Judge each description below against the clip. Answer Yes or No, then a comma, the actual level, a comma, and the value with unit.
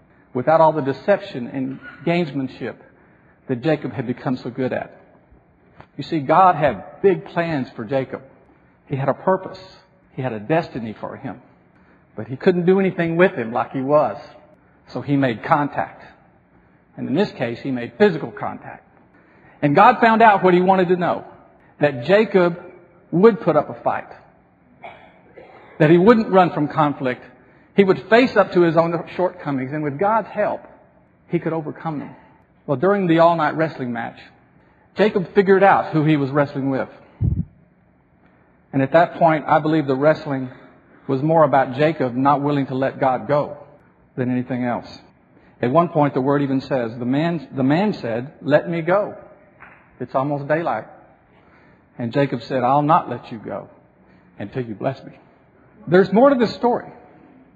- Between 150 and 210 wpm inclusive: Yes, average, 170 wpm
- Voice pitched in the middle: Yes, medium, 150 Hz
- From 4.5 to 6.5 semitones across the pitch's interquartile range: Yes, average, 5.2 semitones